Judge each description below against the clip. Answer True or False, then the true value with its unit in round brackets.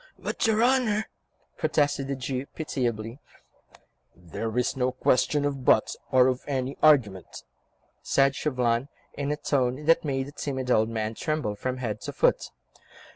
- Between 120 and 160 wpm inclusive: True (150 wpm)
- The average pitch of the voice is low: True (130 Hz)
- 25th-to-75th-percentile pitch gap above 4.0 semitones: False (3.4 semitones)